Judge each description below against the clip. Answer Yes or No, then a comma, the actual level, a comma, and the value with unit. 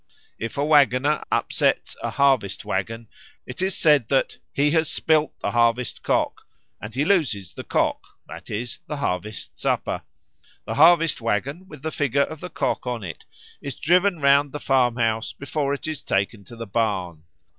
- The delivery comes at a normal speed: Yes, average, 170 wpm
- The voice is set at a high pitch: No, low, 135 Hz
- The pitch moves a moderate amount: Yes, average, 4.9 semitones